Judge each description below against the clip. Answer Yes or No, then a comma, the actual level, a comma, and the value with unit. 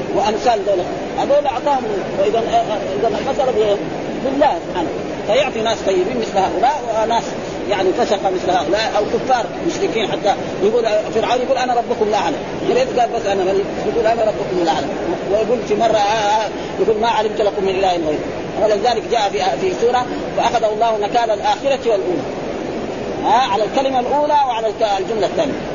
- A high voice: Yes, high, 225 Hz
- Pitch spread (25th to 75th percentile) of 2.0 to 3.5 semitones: Yes, average, 3.1 semitones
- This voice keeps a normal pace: No, fast, 160 wpm